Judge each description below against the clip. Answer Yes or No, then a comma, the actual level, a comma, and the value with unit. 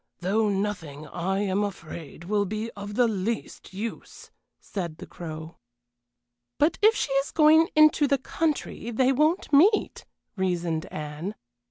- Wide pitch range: Yes, wide, 7.7 semitones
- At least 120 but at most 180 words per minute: Yes, average, 140 wpm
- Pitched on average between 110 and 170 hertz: No, high, 205 Hz